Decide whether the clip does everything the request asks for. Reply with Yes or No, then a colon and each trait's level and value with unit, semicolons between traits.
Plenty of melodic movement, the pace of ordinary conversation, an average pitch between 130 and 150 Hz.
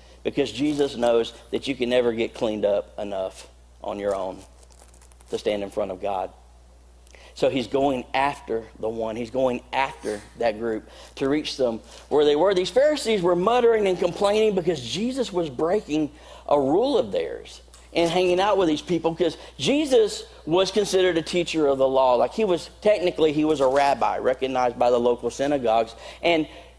Yes: wide, 7.8 semitones; average, 180 wpm; medium, 140 Hz